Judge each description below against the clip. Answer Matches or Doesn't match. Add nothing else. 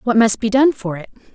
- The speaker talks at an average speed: Doesn't match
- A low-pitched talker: Doesn't match